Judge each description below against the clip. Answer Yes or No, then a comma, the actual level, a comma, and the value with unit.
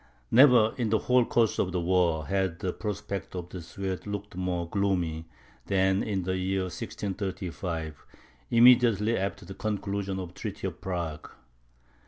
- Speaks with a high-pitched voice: No, very low, 95 Hz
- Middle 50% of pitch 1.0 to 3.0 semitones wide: Yes, narrow, 2.6 semitones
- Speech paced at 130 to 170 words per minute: Yes, average, 155 wpm